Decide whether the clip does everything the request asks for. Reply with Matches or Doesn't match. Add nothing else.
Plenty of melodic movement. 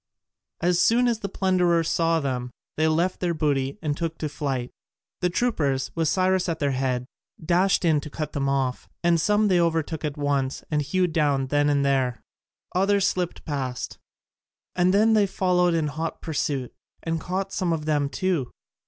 Doesn't match